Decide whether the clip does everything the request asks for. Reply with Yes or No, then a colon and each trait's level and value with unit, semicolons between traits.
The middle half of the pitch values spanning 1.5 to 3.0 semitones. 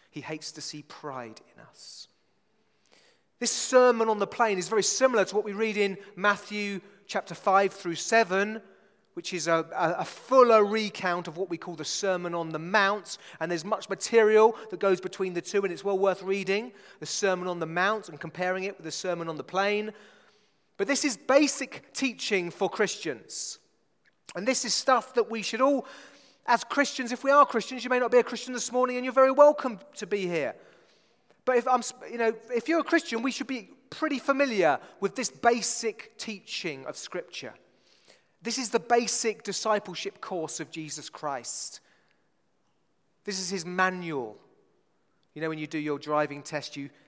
No: average, 5.2 semitones